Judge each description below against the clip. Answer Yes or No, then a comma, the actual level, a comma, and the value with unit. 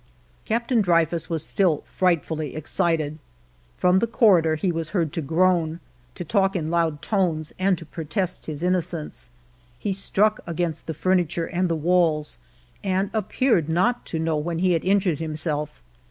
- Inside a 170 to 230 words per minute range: No, average, 155 wpm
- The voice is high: No, medium, 170 Hz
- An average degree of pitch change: Yes, average, 3.0 semitones